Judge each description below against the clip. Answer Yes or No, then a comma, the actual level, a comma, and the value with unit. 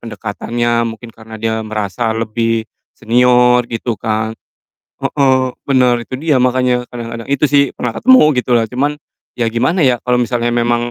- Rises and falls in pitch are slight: Yes, narrow, 1.9 semitones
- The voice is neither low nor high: No, low, 120 Hz